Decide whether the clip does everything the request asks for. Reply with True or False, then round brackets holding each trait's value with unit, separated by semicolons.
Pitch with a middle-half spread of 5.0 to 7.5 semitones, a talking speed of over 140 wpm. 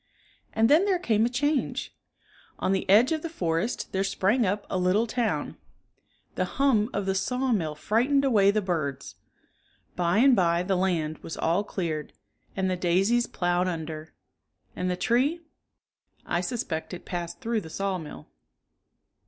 True (5.4 semitones; 155 wpm)